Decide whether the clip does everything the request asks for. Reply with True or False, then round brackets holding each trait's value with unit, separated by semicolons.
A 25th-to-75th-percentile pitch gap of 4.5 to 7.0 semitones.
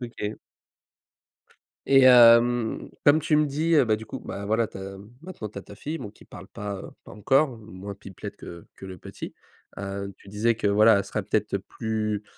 False (4.0 semitones)